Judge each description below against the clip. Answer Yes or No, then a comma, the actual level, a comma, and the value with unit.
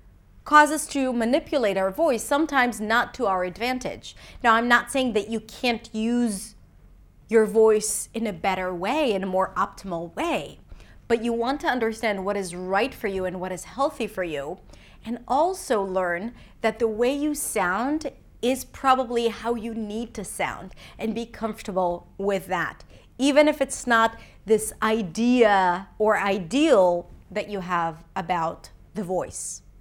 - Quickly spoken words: No, average, 160 wpm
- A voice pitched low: No, high, 225 Hz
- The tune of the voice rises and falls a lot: No, average, 4.1 semitones